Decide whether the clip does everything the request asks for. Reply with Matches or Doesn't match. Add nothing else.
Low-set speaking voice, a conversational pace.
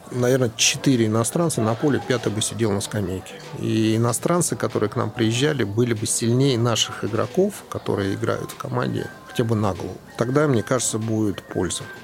Doesn't match